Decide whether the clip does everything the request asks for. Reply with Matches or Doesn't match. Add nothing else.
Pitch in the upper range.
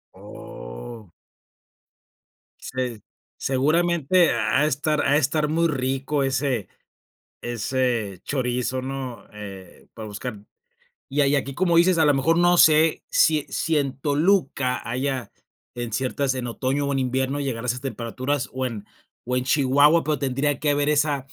Doesn't match